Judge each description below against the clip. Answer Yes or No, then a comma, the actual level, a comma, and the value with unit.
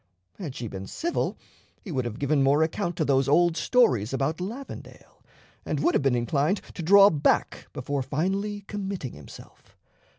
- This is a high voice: No, medium, 155 Hz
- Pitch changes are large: Yes, wide, 6.6 semitones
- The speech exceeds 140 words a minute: Yes, average, 165 wpm